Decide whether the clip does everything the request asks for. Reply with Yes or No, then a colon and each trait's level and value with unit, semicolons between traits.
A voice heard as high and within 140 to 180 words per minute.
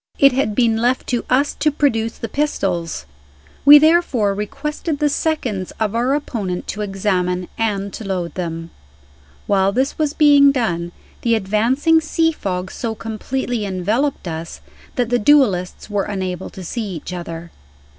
Yes: high, 220 Hz; average, 155 wpm